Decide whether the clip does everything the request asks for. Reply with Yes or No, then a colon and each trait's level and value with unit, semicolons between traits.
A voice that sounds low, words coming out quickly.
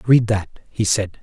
No: low, 105 Hz; average, 195 wpm